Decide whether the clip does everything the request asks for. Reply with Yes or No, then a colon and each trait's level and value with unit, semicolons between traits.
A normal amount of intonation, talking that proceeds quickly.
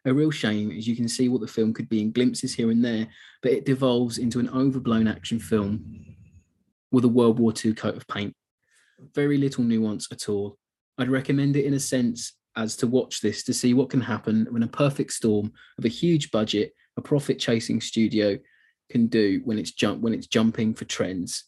Yes: average, 3.0 semitones; fast, 210 wpm